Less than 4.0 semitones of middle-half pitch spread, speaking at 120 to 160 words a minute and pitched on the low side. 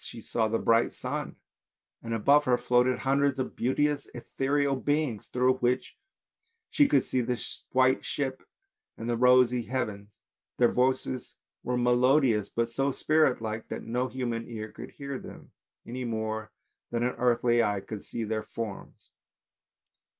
Yes: narrow, 2.4 semitones; average, 150 wpm; low, 125 Hz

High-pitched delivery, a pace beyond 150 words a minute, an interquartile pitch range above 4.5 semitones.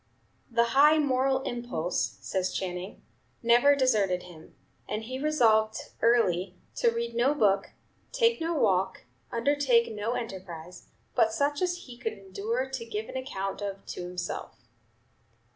No: high, 230 Hz; average, 140 wpm; average, 5.3 semitones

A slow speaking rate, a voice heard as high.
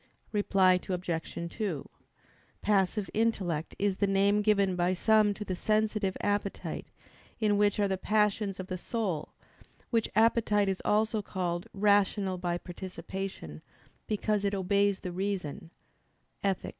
Yes: slow, 130 wpm; high, 200 Hz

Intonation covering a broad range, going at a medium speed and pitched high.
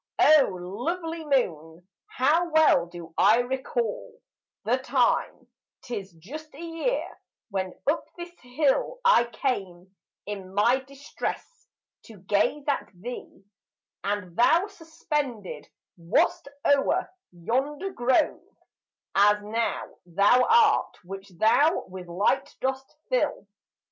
No: wide, 8.0 semitones; slow, 105 wpm; high, 245 Hz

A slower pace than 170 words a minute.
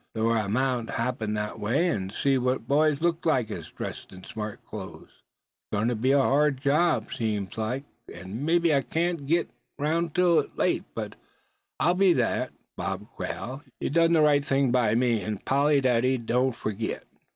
No: average, 185 wpm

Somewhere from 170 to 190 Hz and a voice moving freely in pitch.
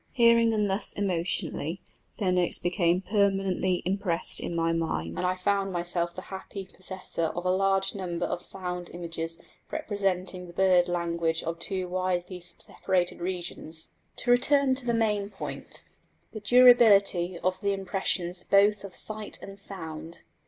No: medium, 185 Hz; narrow, 2.4 semitones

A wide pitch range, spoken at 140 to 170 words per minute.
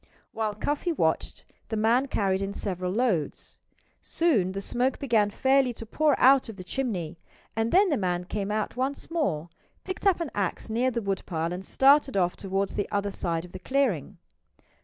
No: wide, 6.0 semitones; average, 180 wpm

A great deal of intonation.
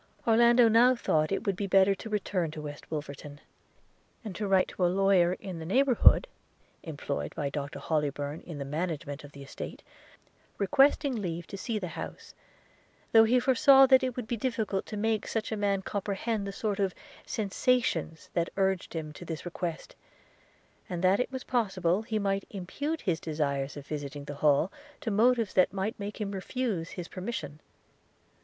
Yes: wide, 5.7 semitones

